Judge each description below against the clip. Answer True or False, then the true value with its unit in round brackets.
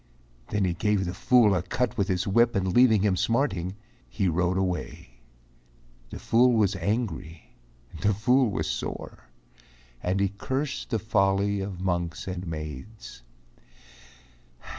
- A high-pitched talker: False (95 Hz)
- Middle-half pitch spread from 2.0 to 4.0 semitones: True (3.6 semitones)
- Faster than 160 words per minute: False (140 wpm)